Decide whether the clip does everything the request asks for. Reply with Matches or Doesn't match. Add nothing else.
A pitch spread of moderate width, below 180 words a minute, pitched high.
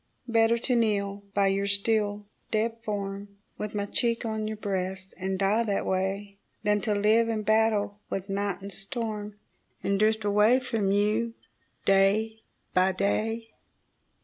Doesn't match